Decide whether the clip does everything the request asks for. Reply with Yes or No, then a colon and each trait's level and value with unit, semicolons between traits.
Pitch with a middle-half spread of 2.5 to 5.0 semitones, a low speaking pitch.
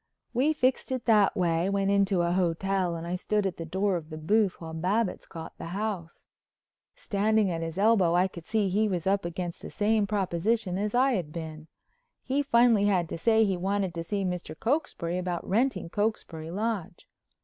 No: average, 3.9 semitones; high, 195 Hz